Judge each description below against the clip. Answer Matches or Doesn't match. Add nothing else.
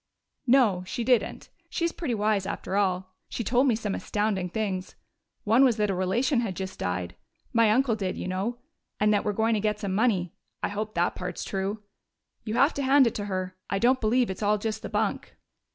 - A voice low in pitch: Doesn't match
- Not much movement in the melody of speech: Doesn't match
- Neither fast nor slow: Doesn't match